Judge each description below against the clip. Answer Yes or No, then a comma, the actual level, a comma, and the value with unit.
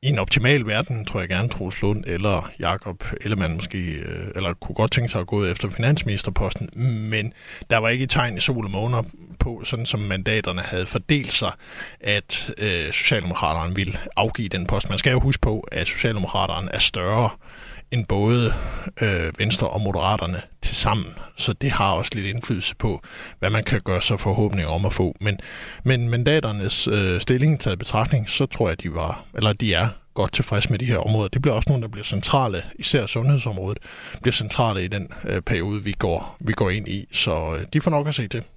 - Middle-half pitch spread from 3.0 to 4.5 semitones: Yes, average, 4.0 semitones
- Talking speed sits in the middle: Yes, average, 200 wpm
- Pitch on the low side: Yes, low, 110 Hz